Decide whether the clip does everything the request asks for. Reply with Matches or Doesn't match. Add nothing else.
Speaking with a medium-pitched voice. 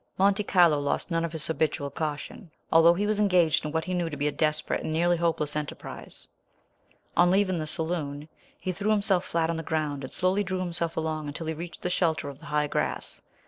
Matches